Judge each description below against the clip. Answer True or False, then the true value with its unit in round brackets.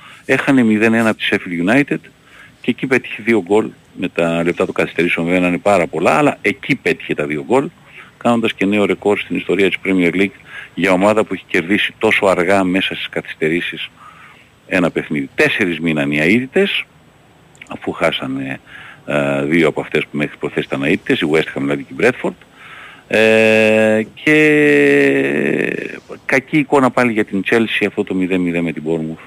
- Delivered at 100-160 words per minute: False (170 wpm)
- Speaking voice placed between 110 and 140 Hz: False (100 Hz)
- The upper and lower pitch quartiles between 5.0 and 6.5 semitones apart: True (5.3 semitones)